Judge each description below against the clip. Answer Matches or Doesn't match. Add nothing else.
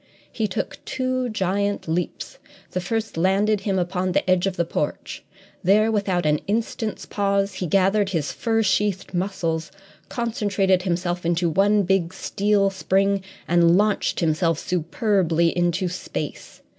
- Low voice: Doesn't match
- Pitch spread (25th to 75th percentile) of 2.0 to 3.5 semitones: Matches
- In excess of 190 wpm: Doesn't match